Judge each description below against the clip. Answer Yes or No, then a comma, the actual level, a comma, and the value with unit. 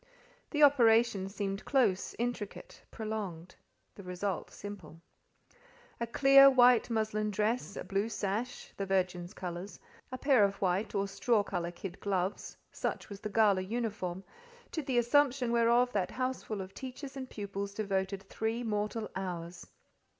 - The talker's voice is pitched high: Yes, high, 210 Hz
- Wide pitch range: No, average, 3.7 semitones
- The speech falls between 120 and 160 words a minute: Yes, average, 140 wpm